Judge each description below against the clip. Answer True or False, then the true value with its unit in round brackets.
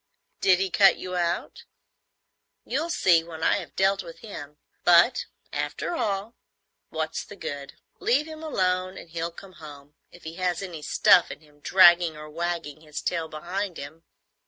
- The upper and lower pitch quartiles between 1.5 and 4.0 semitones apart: True (3.4 semitones)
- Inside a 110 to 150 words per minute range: False (165 wpm)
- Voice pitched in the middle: True (175 Hz)